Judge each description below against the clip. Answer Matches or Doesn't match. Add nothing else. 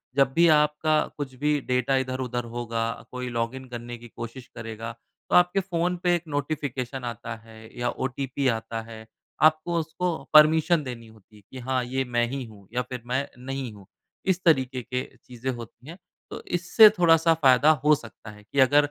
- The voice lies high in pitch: Doesn't match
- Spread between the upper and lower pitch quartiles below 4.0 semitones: Doesn't match